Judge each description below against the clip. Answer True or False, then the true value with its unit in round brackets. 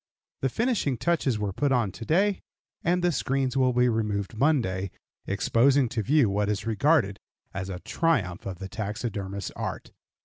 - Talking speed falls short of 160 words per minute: False (165 wpm)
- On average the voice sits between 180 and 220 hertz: False (115 Hz)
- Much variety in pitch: True (5.9 semitones)